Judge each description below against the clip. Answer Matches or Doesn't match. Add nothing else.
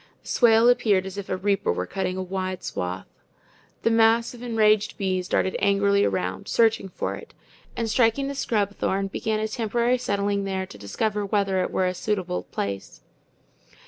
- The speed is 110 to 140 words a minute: Doesn't match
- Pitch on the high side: Matches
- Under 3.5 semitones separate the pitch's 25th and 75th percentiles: Matches